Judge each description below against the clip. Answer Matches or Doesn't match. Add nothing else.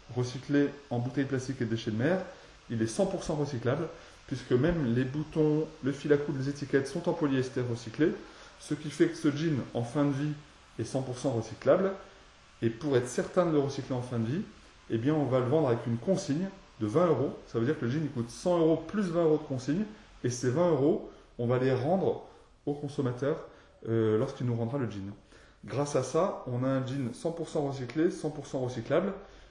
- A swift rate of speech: Doesn't match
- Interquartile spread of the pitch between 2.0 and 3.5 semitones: Doesn't match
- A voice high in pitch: Doesn't match